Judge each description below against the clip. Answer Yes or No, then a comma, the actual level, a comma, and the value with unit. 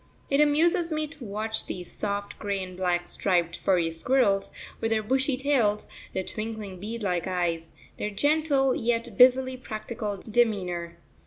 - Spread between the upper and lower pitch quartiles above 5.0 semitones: Yes, wide, 5.6 semitones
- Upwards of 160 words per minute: No, average, 150 wpm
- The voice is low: No, high, 215 Hz